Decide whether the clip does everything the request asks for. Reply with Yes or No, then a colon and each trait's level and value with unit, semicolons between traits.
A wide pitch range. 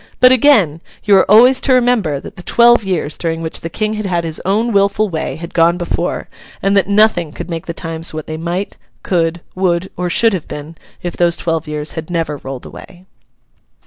No: average, 3.7 semitones